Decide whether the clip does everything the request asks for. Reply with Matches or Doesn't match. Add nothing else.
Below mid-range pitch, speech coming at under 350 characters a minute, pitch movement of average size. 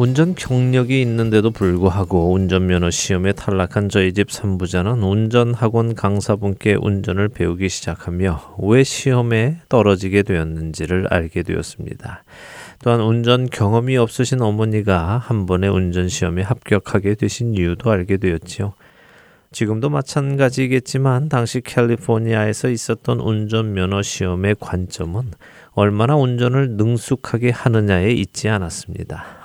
Matches